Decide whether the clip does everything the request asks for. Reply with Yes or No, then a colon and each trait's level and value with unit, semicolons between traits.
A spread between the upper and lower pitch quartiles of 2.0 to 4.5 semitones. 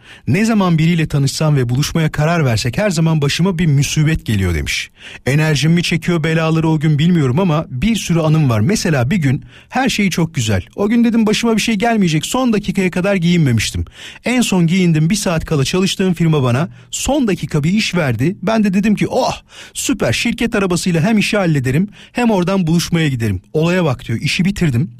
No: average, 5.2 semitones